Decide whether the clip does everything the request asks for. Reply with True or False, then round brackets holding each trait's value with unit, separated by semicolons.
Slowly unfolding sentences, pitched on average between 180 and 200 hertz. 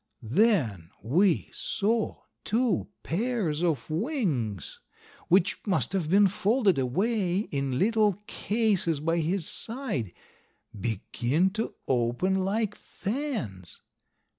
True (100 wpm; 190 Hz)